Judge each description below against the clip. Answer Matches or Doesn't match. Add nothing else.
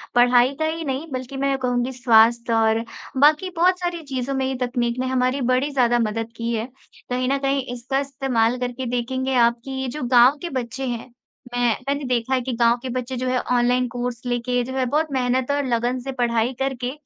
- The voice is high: Matches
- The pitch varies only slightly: Matches